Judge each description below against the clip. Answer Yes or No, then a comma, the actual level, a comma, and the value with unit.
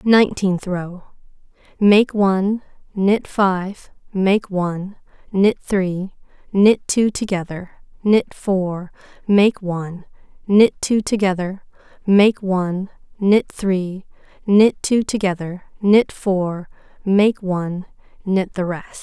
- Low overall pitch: No, high, 195 Hz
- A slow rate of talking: Yes, slow, 105 wpm